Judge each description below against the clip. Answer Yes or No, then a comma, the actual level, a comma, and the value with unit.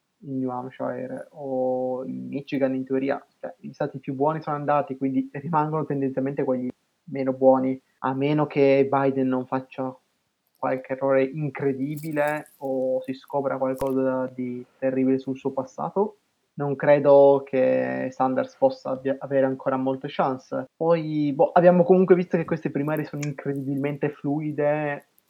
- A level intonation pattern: Yes, narrow, 2.0 semitones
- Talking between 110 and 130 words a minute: No, average, 140 wpm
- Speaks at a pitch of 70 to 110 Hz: No, low, 135 Hz